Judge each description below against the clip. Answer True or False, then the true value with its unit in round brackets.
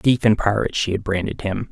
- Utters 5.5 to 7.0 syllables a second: True (6.0 syllables/s)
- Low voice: True (105 Hz)